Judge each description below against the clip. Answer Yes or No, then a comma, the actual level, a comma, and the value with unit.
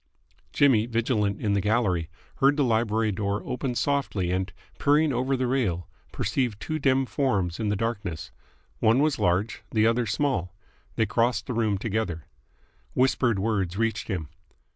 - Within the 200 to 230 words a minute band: No, average, 155 wpm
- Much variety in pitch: No, average, 4.3 semitones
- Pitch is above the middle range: No, low, 110 Hz